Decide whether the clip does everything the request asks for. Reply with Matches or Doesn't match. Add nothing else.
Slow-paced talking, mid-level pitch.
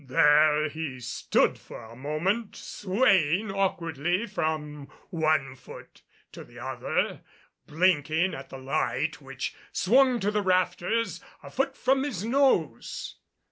Matches